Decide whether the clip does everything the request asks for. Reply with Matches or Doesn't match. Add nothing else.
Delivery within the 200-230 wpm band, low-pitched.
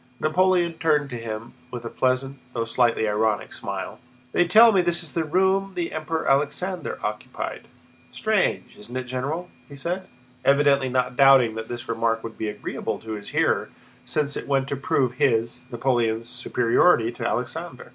Doesn't match